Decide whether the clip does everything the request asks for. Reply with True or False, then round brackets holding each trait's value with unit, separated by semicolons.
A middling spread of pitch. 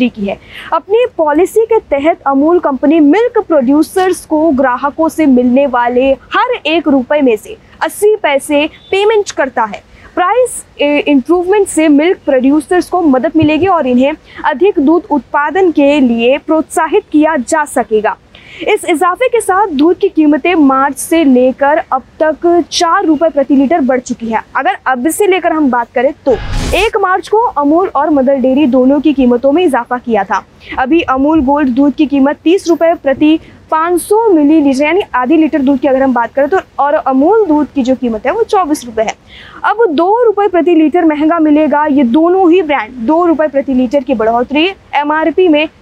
True (4.2 semitones)